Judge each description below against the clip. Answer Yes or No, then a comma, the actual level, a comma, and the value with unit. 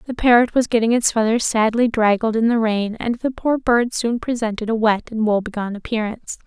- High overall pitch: Yes, high, 225 Hz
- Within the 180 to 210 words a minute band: Yes, fast, 205 wpm